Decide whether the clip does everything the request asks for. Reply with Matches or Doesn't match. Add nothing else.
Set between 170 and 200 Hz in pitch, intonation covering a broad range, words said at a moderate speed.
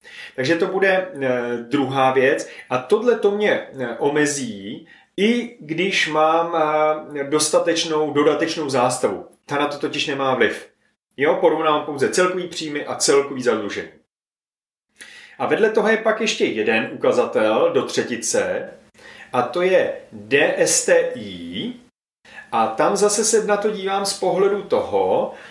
Matches